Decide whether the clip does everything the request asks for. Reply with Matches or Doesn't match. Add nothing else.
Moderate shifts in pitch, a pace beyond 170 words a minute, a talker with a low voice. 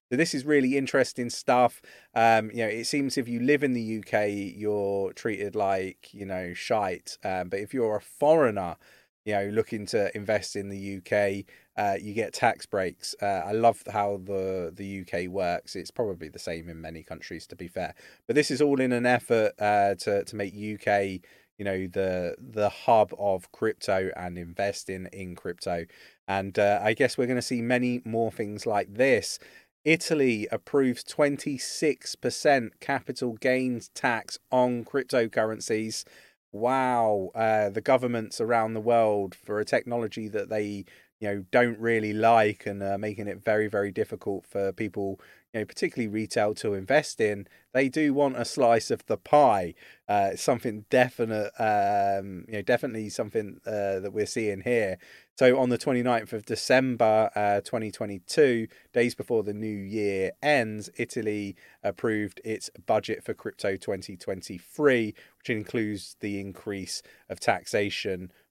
Doesn't match